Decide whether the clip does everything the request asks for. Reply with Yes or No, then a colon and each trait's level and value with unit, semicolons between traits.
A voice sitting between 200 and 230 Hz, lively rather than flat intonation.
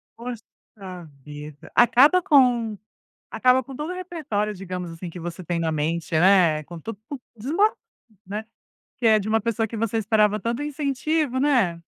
Yes: high, 220 Hz; wide, 6.2 semitones